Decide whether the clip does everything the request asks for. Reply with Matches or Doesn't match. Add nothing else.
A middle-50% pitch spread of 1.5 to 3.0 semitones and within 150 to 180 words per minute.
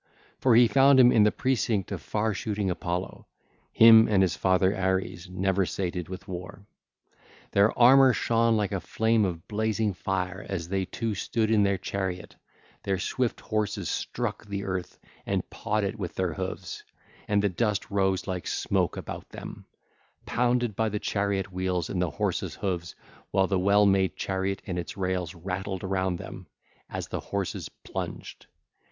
Matches